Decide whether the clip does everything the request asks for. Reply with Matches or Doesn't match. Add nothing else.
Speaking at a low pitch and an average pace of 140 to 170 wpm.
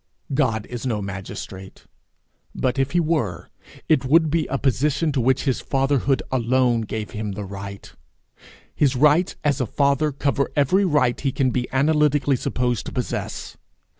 Matches